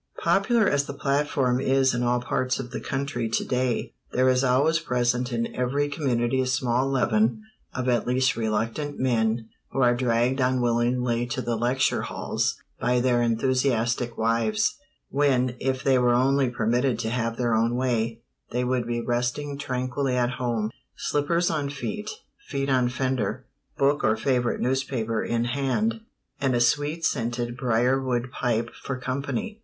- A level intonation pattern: Yes, narrow, 2.1 semitones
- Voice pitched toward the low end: Yes, low, 125 Hz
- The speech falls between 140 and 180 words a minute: Yes, average, 160 wpm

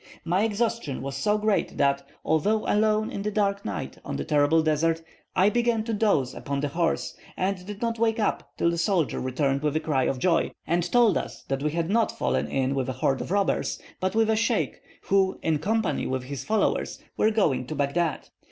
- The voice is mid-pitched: Yes, medium, 170 Hz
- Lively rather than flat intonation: Yes, wide, 7.0 semitones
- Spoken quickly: Yes, fast, 210 wpm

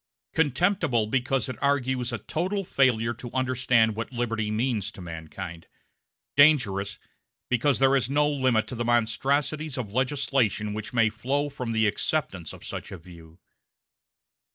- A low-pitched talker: Yes, low, 120 Hz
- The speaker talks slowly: No, average, 145 wpm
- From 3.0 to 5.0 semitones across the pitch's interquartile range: Yes, average, 4.1 semitones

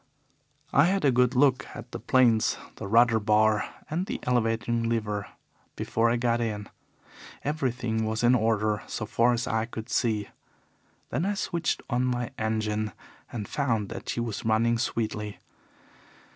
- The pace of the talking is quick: No, average, 155 wpm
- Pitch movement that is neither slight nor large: No, narrow, 2.3 semitones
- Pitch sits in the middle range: No, low, 115 Hz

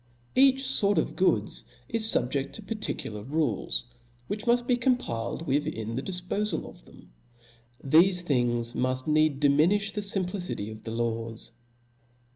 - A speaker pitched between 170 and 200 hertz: No, medium, 155 Hz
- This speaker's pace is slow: No, average, 150 wpm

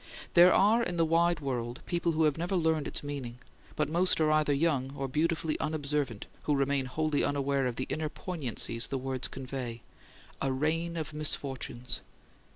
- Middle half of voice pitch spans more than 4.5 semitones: No, average, 3.4 semitones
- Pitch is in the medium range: Yes, medium, 145 Hz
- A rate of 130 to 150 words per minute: No, average, 170 wpm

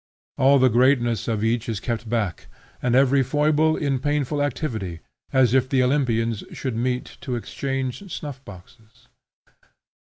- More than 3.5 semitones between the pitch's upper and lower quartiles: No, average, 3.2 semitones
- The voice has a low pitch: Yes, low, 125 Hz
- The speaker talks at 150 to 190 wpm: No, average, 140 wpm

